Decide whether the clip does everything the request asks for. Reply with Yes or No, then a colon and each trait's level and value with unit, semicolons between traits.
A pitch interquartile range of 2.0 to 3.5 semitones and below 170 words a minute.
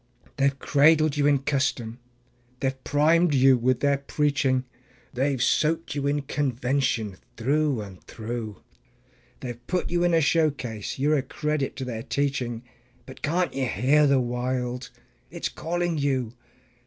Yes: average, 3.1 semitones; average, 155 wpm